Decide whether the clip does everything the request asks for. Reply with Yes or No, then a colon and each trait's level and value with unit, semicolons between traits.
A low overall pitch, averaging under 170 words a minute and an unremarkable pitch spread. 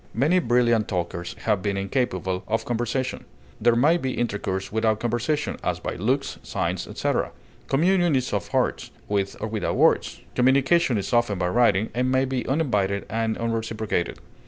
Yes: low, 115 Hz; average, 160 wpm; average, 4.2 semitones